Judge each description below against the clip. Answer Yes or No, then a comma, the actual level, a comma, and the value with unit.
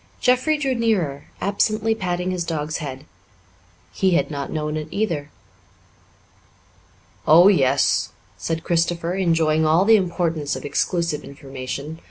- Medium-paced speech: No, slow, 125 wpm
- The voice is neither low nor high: Yes, medium, 165 Hz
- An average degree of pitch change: Yes, average, 4.0 semitones